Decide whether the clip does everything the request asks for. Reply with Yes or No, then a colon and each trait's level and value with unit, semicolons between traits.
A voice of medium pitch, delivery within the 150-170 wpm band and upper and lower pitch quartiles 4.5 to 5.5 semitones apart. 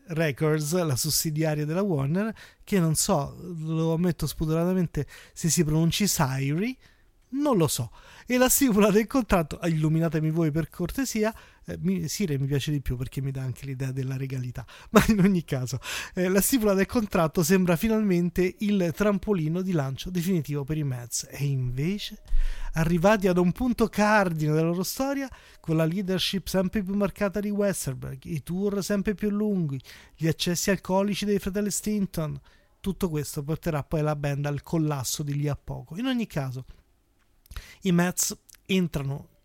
Yes: medium, 170 Hz; average, 160 wpm; average, 5.2 semitones